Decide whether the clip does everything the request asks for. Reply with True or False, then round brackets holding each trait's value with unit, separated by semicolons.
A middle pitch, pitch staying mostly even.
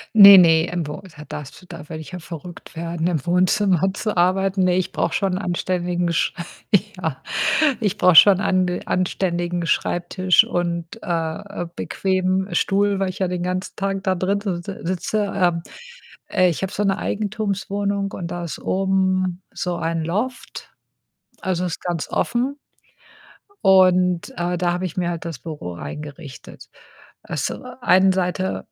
True (180 Hz; 2.0 semitones)